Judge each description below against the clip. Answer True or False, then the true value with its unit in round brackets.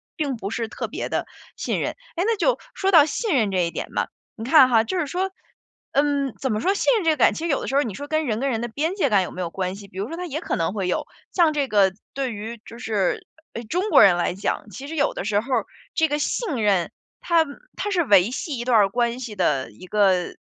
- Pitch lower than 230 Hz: False (240 Hz)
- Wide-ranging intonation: True (7.3 semitones)